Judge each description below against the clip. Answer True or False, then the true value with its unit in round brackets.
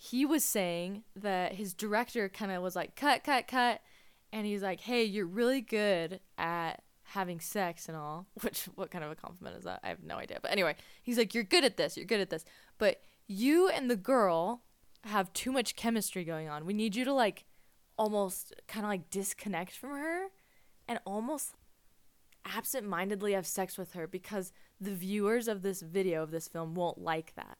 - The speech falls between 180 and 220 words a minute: True (200 wpm)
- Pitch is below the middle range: False (200 Hz)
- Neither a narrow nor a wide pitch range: True (4.4 semitones)